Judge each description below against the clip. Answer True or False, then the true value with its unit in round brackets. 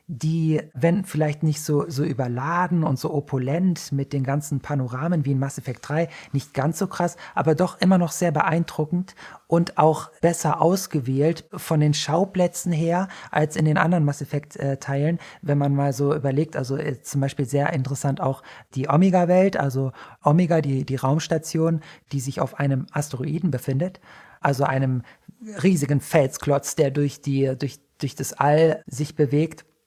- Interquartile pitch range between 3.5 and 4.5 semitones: False (3.1 semitones)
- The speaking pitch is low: False (150 Hz)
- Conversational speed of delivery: True (165 wpm)